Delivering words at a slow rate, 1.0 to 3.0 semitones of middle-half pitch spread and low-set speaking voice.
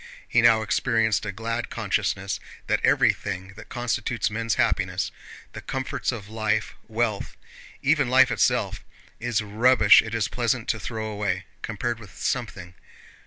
Yes: slow, 130 wpm; narrow, 2.4 semitones; low, 110 Hz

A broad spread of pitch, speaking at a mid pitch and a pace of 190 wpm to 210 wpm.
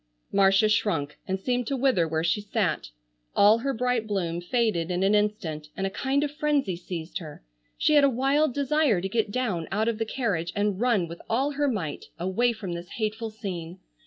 No: wide, 5.9 semitones; high, 210 Hz; average, 200 wpm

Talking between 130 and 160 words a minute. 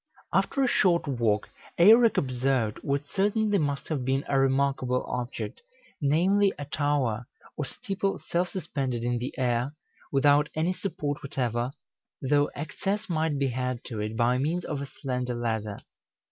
Yes: average, 150 wpm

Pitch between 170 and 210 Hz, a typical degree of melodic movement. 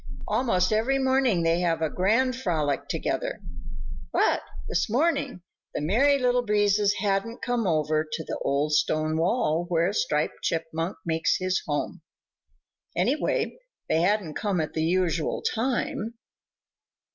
No: medium, 185 Hz; wide, 6.2 semitones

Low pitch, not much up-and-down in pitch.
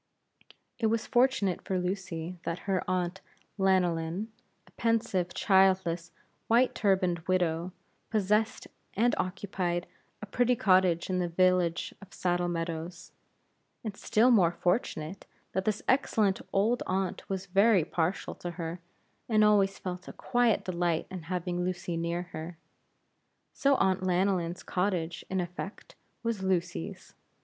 No: medium, 185 Hz; narrow, 2.3 semitones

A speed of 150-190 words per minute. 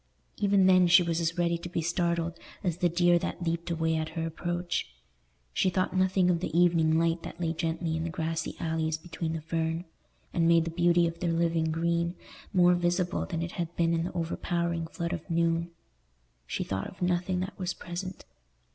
No: average, 200 wpm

